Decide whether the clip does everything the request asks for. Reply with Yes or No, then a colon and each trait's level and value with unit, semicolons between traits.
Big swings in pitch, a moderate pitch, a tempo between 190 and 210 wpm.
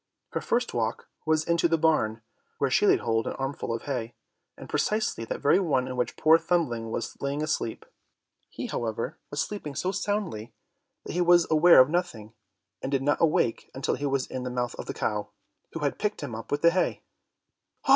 Yes: wide, 5.9 semitones; medium, 145 Hz; fast, 205 wpm